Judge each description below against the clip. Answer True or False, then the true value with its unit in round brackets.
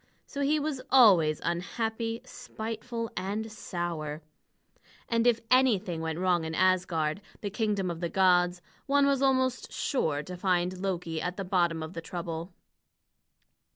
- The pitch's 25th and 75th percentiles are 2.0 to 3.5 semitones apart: False (5.1 semitones)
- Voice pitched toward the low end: False (185 Hz)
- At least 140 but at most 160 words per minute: True (145 wpm)